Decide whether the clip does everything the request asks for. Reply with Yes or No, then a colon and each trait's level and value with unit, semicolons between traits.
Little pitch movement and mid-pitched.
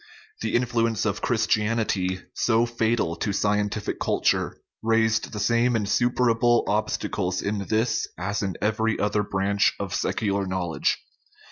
No: narrow, 2.3 semitones; low, 110 Hz